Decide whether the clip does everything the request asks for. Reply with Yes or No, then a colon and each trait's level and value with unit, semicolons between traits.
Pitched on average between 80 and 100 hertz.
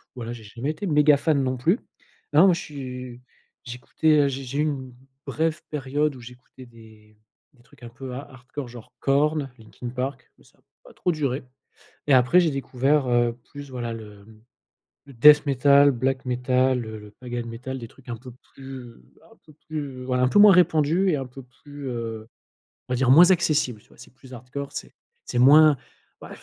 No: low, 130 Hz